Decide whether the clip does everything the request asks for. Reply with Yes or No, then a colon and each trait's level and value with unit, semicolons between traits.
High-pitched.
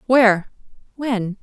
Yes: high, 225 Hz